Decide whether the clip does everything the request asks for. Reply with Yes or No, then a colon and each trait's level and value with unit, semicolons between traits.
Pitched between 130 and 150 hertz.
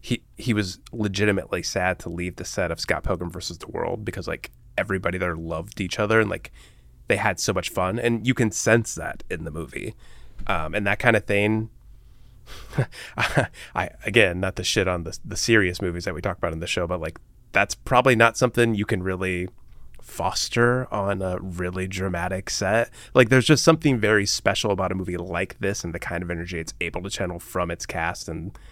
No: low, 100 Hz